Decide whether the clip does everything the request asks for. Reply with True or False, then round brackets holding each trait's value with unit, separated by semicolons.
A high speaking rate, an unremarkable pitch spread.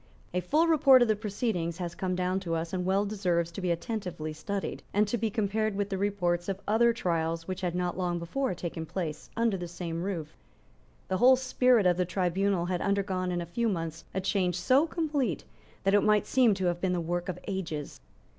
True (215 wpm; 3.3 semitones)